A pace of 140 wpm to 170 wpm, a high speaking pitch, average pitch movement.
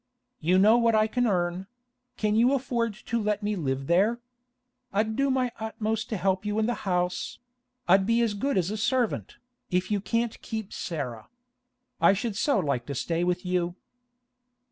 No: average, 180 wpm; high, 210 Hz; average, 4.2 semitones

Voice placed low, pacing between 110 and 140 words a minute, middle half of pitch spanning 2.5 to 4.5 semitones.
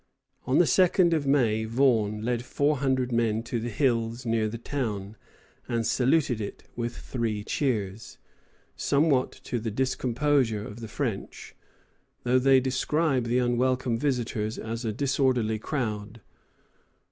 Yes: low, 120 Hz; slow, 135 wpm; average, 3.0 semitones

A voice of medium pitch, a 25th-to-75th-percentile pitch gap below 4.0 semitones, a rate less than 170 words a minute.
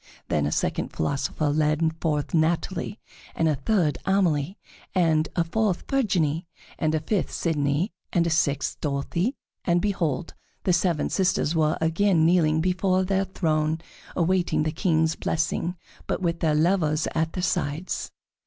Yes: medium, 165 Hz; average, 3.0 semitones; average, 145 wpm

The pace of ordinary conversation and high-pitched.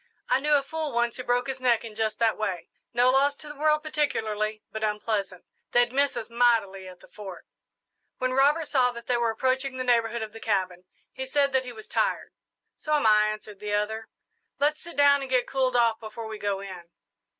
No: fast, 215 wpm; high, 235 Hz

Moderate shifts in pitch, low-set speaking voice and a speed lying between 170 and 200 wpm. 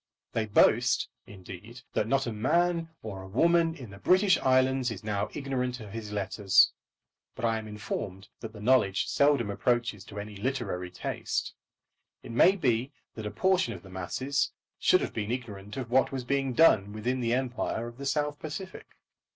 Yes: average, 4.7 semitones; low, 120 Hz; average, 180 wpm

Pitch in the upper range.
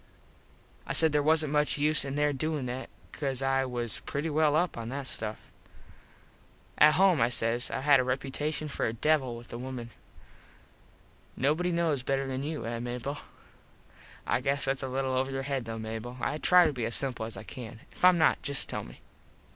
No: low, 135 Hz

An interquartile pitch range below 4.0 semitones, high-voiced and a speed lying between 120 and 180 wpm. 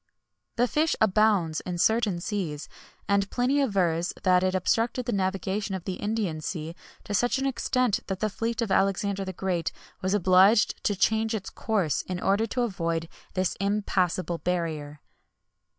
Yes: average, 3.4 semitones; high, 195 Hz; average, 165 wpm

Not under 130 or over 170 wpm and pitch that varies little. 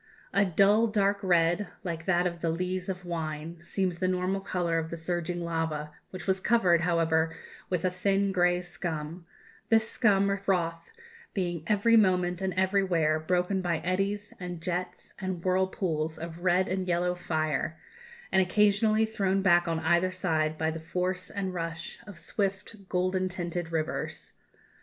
Yes: average, 160 wpm; narrow, 2.3 semitones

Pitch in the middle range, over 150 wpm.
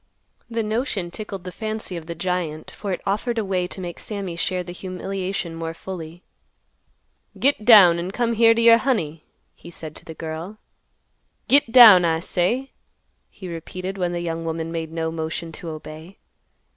Yes: medium, 180 Hz; average, 175 wpm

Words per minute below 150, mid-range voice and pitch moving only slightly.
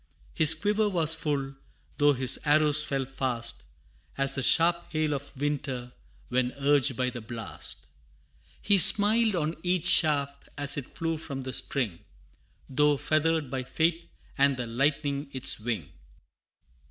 No: average, 140 wpm; medium, 145 Hz; average, 3.3 semitones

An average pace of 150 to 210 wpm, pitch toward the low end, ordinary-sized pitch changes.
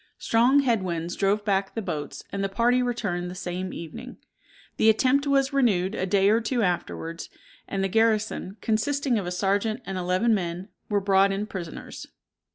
No: average, 175 wpm; high, 200 Hz; average, 3.8 semitones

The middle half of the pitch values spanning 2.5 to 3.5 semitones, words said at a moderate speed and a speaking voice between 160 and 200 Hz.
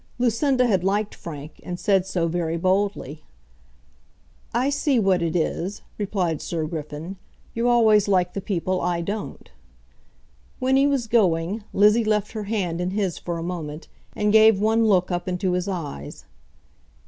No: average, 4.0 semitones; average, 160 wpm; high, 190 Hz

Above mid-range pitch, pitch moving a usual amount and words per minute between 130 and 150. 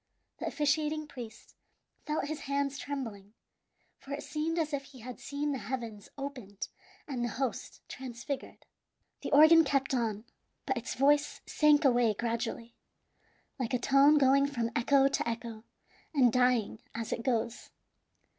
Yes: very high, 265 Hz; average, 3.4 semitones; average, 145 wpm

